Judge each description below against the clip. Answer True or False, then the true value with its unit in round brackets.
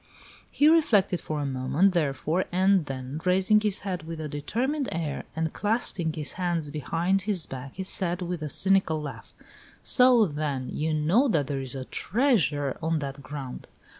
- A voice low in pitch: False (165 Hz)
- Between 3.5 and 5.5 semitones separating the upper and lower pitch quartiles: True (5.0 semitones)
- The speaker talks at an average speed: True (170 wpm)